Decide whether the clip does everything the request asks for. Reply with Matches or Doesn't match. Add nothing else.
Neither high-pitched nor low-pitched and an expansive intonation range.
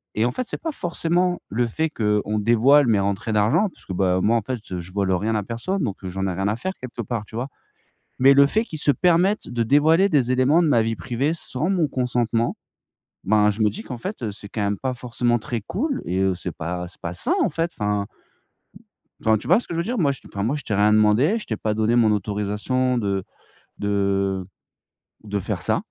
Doesn't match